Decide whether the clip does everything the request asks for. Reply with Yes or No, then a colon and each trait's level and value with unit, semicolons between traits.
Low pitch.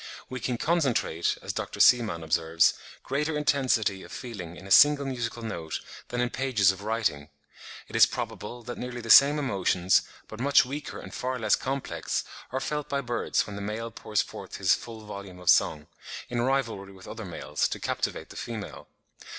Yes: low, 115 Hz